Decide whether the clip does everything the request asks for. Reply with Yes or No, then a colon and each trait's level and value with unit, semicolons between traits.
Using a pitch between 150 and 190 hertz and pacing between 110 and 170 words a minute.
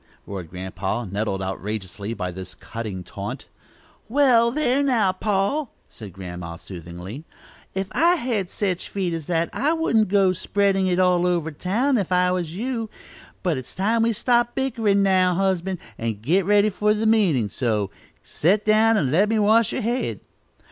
Yes: medium, 185 Hz; average, 165 wpm